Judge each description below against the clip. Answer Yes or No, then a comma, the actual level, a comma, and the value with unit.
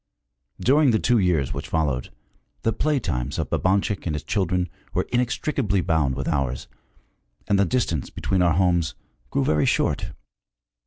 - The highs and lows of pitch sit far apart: Yes, wide, 6.8 semitones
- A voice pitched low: Yes, very low, 90 Hz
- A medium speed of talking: Yes, average, 155 wpm